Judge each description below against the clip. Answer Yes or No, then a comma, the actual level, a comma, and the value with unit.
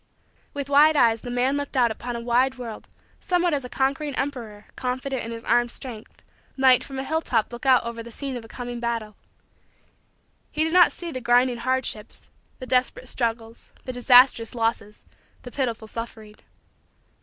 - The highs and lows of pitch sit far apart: No, narrow, 2.5 semitones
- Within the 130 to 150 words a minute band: No, average, 175 wpm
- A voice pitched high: Yes, high, 245 Hz